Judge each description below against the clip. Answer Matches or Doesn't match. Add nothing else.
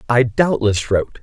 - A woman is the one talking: Doesn't match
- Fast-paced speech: Doesn't match